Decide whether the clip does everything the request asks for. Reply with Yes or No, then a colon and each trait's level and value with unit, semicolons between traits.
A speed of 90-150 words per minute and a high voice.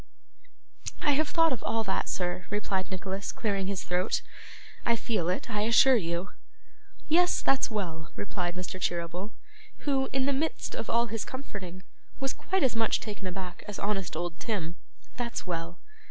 No: average, 165 wpm; high, 200 Hz